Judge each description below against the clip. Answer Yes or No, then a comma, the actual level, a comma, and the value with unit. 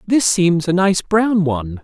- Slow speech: No, average, 195 wpm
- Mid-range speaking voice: Yes, medium, 180 Hz